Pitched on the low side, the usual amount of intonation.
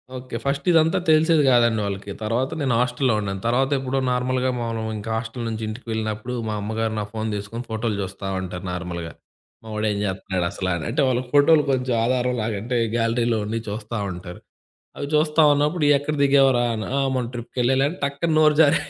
Yes: low, 120 Hz; average, 3.7 semitones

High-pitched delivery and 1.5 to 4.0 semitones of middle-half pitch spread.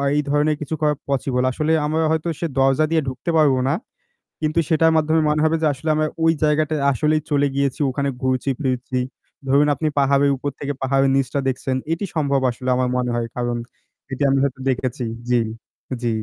No: medium, 140 Hz; average, 2.9 semitones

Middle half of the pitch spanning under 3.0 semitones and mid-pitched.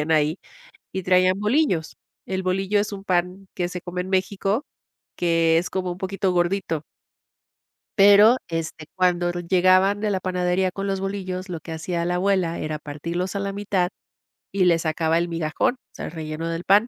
Yes: narrow, 2.5 semitones; medium, 180 Hz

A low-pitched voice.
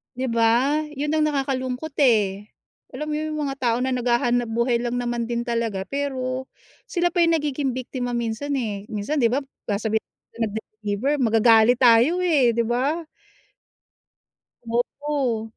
No: high, 245 Hz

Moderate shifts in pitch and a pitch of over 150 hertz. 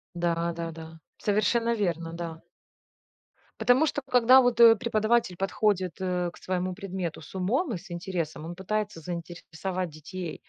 Yes: average, 4.2 semitones; medium, 185 Hz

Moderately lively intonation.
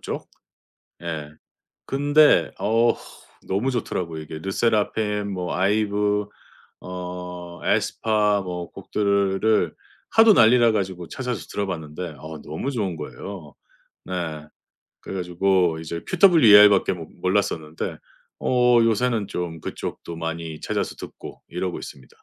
Yes: average, 4.3 semitones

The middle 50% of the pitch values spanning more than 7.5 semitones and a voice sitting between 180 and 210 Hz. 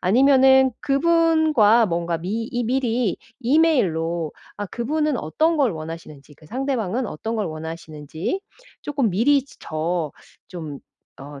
No: wide, 8.7 semitones; high, 225 Hz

